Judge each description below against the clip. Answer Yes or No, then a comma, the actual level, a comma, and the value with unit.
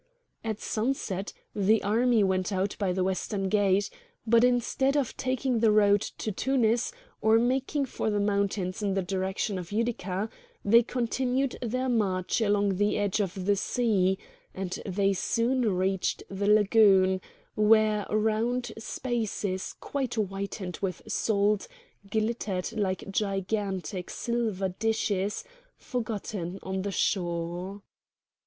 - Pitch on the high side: Yes, high, 205 Hz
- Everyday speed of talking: No, slow, 125 wpm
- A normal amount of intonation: Yes, average, 3.0 semitones